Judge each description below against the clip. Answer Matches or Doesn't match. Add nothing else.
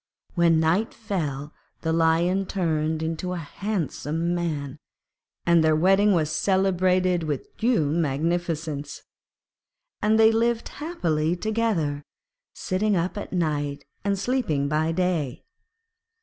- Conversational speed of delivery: Doesn't match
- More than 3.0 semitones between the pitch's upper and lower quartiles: Matches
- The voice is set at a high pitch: Doesn't match